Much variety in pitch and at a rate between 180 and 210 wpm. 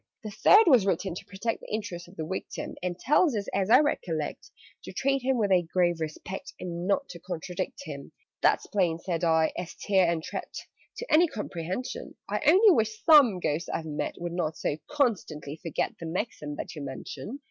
Yes: wide, 5.8 semitones; average, 195 wpm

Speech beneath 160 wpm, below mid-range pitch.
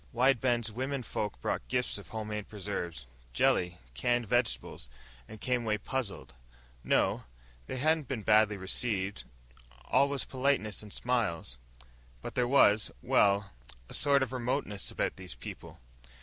Yes: average, 140 wpm; low, 110 Hz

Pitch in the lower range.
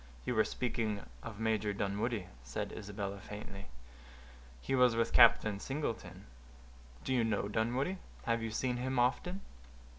Yes: low, 115 Hz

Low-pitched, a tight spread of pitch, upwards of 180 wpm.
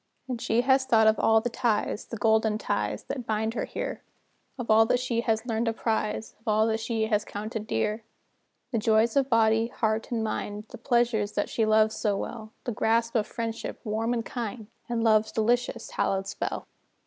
No: high, 225 Hz; narrow, 1.3 semitones; average, 195 wpm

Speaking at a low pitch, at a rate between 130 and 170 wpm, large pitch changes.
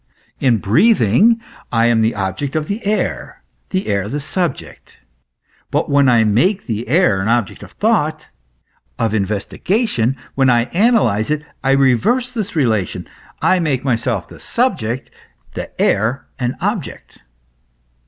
Yes: low, 130 Hz; average, 140 wpm; wide, 8.5 semitones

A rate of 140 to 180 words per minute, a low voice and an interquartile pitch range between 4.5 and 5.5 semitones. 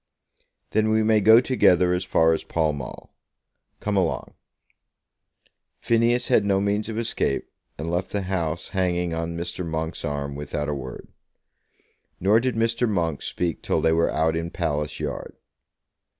Yes: average, 155 wpm; very low, 90 Hz; average, 4.9 semitones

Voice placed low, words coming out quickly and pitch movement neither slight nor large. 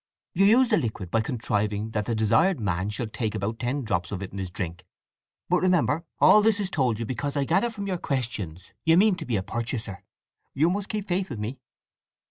No: low, 120 Hz; fast, 225 wpm; wide, 9.0 semitones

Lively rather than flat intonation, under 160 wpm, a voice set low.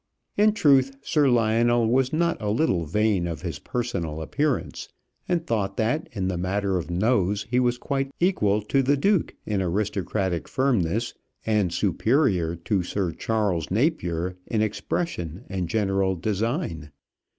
Yes: wide, 5.9 semitones; average, 145 wpm; low, 105 Hz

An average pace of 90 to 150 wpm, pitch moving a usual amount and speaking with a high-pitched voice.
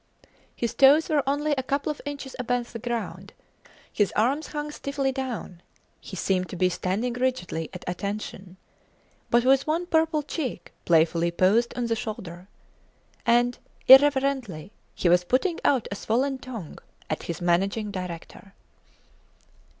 No: average, 140 wpm; wide, 6.7 semitones; high, 235 Hz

